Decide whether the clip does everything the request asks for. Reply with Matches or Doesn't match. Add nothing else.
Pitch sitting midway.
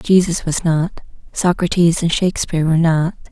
Matches